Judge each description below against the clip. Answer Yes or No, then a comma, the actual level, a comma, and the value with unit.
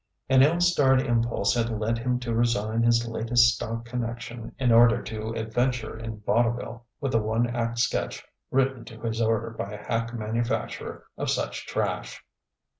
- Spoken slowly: No, average, 165 wpm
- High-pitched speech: No, low, 115 Hz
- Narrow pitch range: Yes, narrow, 1.2 semitones